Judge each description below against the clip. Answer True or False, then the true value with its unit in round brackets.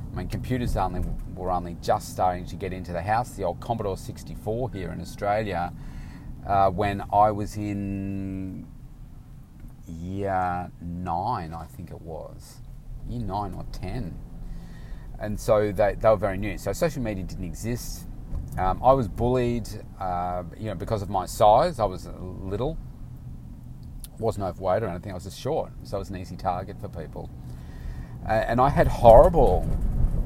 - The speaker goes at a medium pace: True (165 wpm)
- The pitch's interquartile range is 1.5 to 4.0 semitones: True (3.4 semitones)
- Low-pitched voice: True (95 Hz)